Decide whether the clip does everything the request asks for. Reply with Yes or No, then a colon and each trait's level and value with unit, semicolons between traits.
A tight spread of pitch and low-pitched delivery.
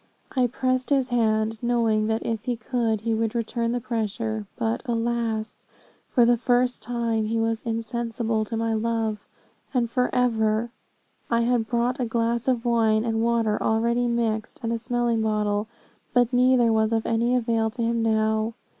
No: narrow, 1.4 semitones; high, 230 Hz